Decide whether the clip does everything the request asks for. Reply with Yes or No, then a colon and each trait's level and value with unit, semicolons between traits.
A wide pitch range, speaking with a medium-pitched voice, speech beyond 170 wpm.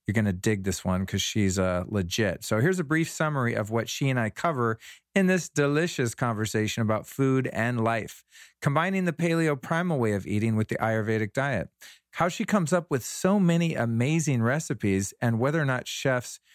No: wide, 6.5 semitones; low, 120 Hz; average, 195 wpm